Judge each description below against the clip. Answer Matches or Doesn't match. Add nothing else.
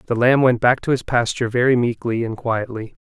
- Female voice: Doesn't match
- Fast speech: Matches